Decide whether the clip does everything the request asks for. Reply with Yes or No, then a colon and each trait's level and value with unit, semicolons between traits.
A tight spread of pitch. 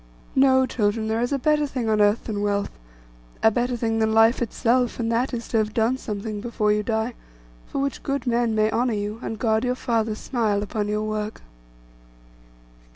Yes: narrow, 2.3 semitones